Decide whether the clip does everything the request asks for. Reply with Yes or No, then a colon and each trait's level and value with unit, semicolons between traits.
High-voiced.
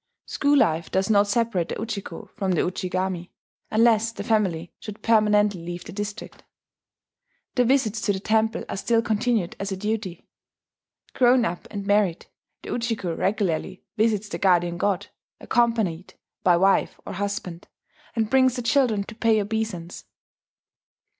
Yes: high, 205 Hz